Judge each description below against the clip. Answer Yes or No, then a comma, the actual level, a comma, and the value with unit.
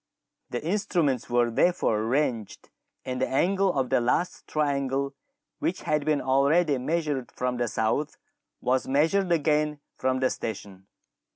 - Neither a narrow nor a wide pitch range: Yes, average, 3.7 semitones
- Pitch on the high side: No, medium, 140 Hz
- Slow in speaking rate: Yes, slow, 130 wpm